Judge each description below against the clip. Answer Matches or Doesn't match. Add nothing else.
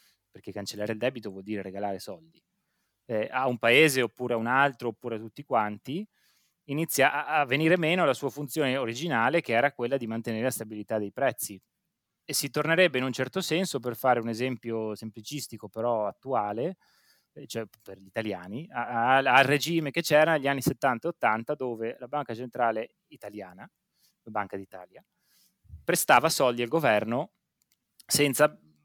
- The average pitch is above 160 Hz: Doesn't match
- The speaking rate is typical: Matches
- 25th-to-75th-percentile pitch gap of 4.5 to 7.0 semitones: Matches